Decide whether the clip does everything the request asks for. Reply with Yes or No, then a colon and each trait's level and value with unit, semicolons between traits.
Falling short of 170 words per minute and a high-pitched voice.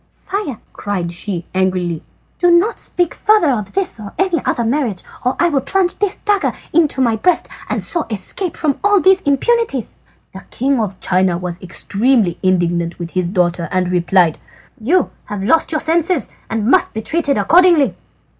No: average, 175 wpm; high, 240 Hz